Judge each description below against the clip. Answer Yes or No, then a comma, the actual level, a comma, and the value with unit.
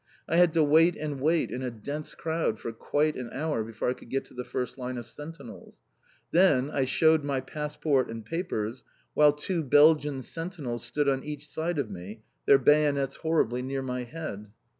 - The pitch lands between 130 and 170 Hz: Yes, medium, 140 Hz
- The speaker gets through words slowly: No, average, 190 wpm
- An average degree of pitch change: Yes, average, 3.7 semitones